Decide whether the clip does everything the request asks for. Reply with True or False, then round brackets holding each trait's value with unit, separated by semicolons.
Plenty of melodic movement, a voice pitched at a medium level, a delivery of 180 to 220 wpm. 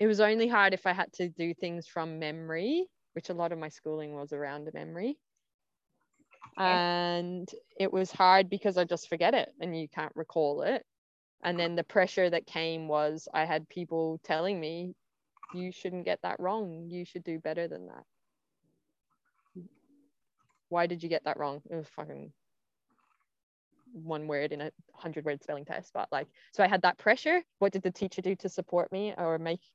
False (2.9 semitones; 175 Hz; 190 wpm)